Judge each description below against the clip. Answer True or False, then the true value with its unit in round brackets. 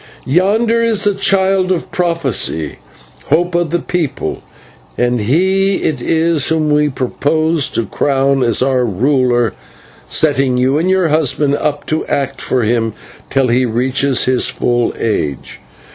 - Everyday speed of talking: True (145 wpm)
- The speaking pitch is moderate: True (145 Hz)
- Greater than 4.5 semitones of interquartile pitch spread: True (5.4 semitones)